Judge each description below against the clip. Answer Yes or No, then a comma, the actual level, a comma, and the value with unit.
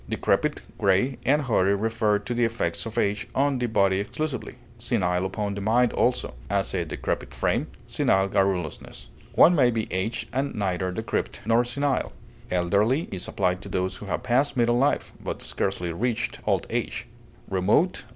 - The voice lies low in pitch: Yes, low, 105 Hz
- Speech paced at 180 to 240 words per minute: No, average, 170 wpm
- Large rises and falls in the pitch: No, average, 4.4 semitones